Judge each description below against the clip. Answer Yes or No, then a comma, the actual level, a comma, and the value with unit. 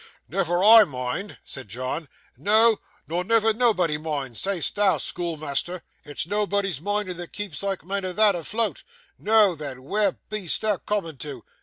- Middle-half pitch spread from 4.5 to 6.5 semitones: Yes, wide, 5.4 semitones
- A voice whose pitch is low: No, medium, 185 Hz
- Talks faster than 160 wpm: No, average, 155 wpm